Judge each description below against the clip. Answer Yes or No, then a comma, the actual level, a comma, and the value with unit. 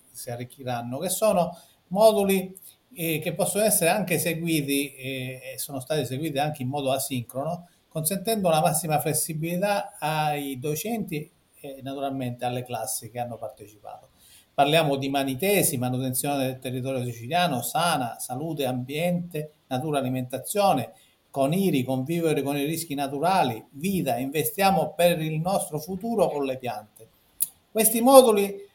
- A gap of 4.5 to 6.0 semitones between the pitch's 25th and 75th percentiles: Yes, average, 4.9 semitones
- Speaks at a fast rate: No, average, 135 wpm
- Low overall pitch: No, medium, 150 Hz